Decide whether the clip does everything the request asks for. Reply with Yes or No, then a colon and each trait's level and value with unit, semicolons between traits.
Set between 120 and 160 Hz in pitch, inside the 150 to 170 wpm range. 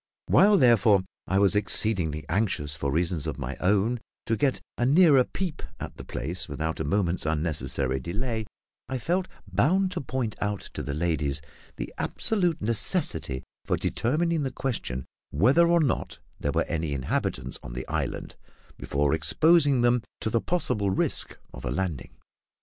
No: low, 105 Hz; average, 160 wpm